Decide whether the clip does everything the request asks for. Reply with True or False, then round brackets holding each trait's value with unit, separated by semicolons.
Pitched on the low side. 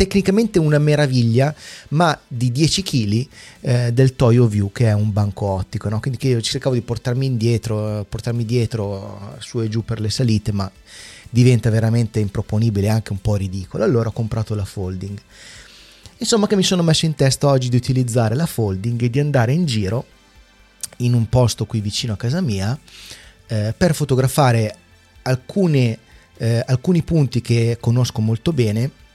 True (115 Hz)